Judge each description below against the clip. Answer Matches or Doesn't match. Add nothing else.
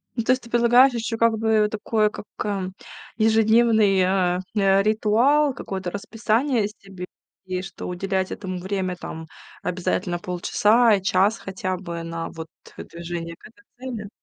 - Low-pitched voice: Doesn't match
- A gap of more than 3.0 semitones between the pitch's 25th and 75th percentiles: Matches